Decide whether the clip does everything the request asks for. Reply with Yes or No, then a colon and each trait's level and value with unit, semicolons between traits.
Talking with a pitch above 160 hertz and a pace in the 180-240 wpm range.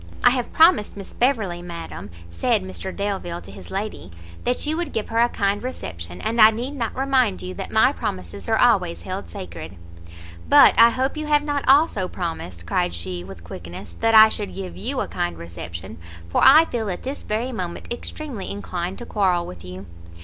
Yes: high, 190 Hz; average, 195 wpm